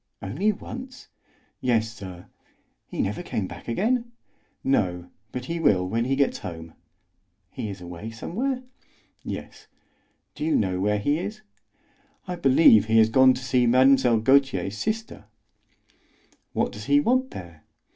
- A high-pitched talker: No, low, 125 Hz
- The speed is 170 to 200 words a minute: No, average, 145 wpm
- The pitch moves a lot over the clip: Yes, wide, 8.8 semitones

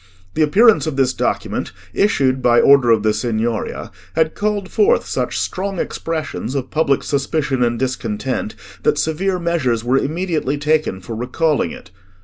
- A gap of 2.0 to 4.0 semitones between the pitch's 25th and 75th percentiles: No, average, 5.1 semitones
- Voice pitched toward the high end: No, medium, 140 Hz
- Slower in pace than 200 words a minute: Yes, average, 150 wpm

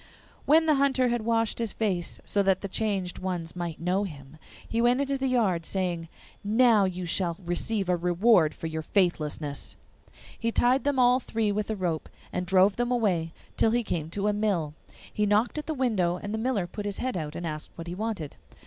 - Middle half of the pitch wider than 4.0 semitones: Yes, average, 4.9 semitones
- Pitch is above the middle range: Yes, high, 200 Hz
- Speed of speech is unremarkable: No, fast, 210 wpm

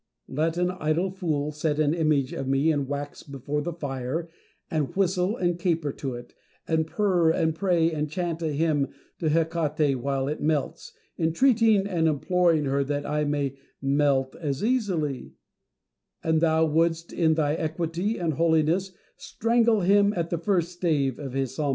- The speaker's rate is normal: Yes, average, 170 wpm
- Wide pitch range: No, average, 3.3 semitones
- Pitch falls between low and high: Yes, medium, 160 Hz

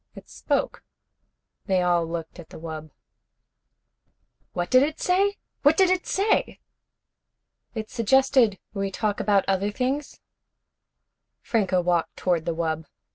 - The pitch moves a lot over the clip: Yes, wide, 7.4 semitones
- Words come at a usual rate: No, slow, 130 wpm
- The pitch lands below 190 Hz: No, high, 200 Hz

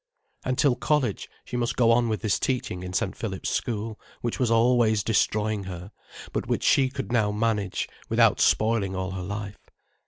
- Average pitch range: Yes, average, 3.0 semitones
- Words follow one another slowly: No, average, 180 wpm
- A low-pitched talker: Yes, low, 110 Hz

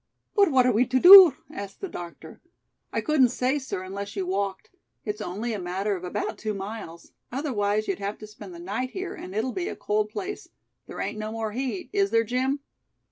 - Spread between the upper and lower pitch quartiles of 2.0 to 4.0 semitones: No, average, 4.6 semitones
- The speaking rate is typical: No, fast, 210 wpm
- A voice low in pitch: No, high, 215 Hz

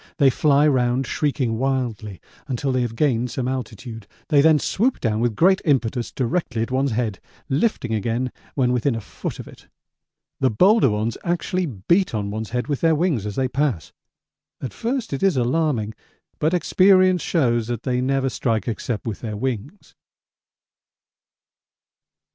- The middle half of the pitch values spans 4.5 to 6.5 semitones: Yes, average, 4.8 semitones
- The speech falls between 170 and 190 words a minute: No, average, 160 wpm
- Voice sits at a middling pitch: No, low, 130 Hz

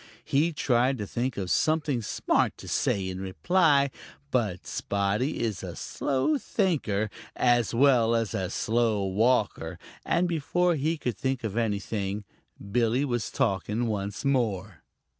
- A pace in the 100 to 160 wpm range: Yes, average, 140 wpm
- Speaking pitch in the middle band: No, low, 120 Hz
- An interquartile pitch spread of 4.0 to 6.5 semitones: Yes, average, 5.2 semitones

